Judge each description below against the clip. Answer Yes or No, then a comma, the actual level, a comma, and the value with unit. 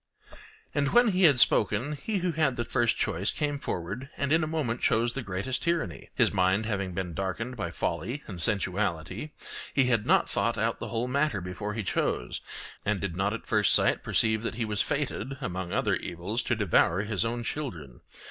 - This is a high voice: No, low, 110 Hz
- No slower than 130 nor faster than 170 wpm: No, average, 195 wpm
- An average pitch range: No, wide, 5.9 semitones